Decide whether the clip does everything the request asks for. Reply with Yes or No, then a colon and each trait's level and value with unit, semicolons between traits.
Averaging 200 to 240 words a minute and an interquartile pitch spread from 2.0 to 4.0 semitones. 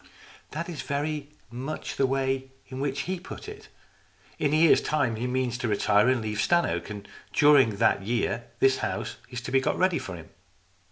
No: fast, 205 wpm; average, 4.4 semitones